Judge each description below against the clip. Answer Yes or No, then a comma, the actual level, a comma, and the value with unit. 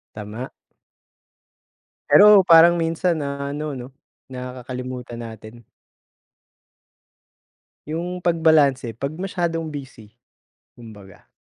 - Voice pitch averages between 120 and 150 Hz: Yes, medium, 140 Hz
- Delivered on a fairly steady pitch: No, average, 5.2 semitones